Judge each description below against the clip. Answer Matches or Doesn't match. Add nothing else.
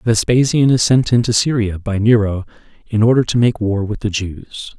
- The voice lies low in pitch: Matches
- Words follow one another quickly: Doesn't match